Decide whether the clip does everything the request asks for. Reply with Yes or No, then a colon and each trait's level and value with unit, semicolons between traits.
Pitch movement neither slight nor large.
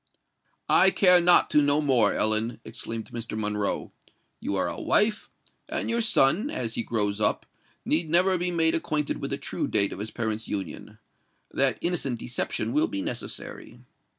No: wide, 8.4 semitones